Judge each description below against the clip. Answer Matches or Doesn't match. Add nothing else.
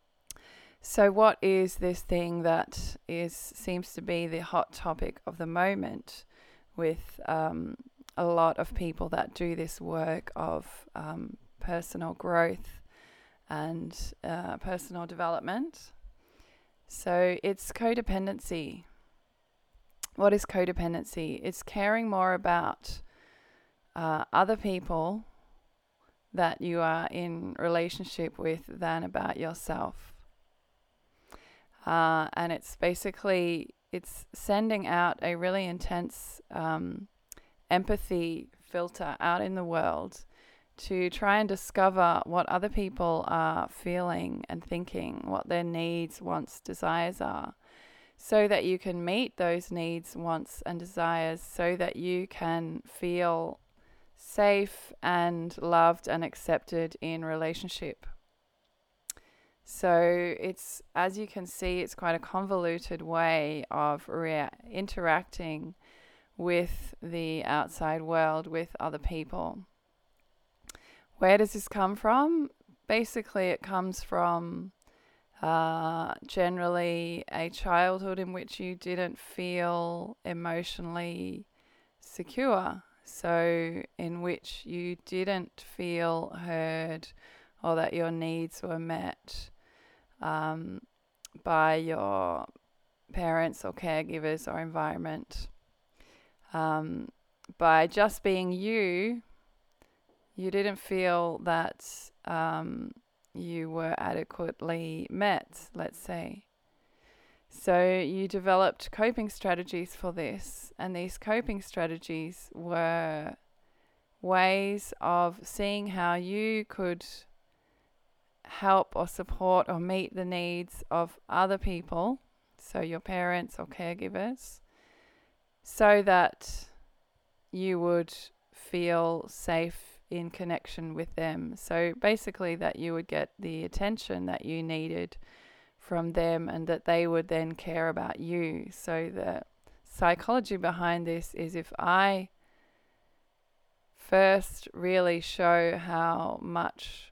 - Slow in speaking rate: Matches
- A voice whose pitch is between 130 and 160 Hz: Doesn't match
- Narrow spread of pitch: Matches